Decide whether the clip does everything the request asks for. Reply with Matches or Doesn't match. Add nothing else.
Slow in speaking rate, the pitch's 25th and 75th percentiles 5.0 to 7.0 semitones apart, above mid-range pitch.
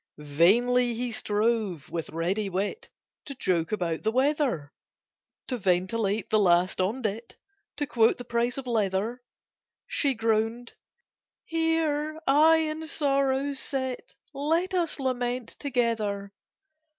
Matches